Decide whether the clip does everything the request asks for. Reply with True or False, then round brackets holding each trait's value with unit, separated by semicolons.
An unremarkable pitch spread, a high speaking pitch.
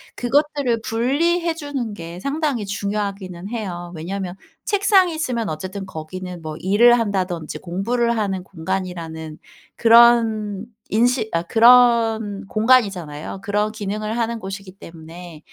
True (4.5 semitones; 210 Hz)